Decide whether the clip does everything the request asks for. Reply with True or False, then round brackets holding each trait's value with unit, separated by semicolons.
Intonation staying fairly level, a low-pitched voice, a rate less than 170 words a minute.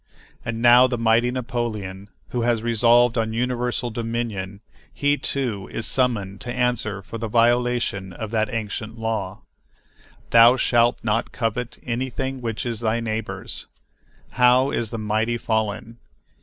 True (1.9 semitones; 115 Hz; 140 wpm)